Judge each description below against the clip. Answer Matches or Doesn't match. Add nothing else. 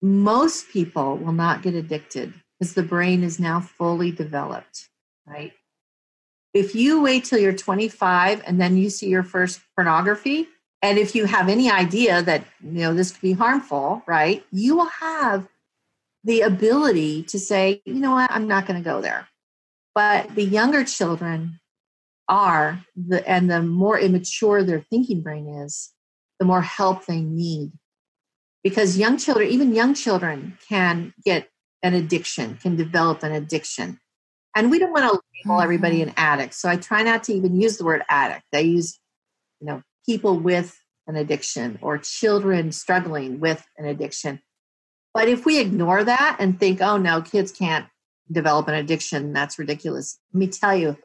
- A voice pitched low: Doesn't match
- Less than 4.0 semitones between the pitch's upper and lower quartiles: Doesn't match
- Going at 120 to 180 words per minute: Matches